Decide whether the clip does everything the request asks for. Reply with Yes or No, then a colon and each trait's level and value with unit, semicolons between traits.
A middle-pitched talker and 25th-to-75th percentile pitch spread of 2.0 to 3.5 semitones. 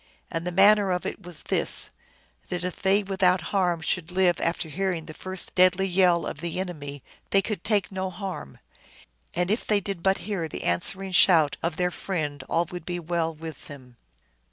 Yes: medium, 180 Hz; average, 2.7 semitones